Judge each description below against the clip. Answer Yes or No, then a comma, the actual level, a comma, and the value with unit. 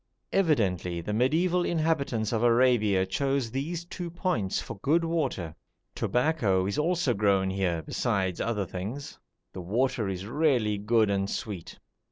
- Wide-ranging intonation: Yes, wide, 7.4 semitones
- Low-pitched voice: Yes, low, 115 Hz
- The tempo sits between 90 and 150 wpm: Yes, average, 140 wpm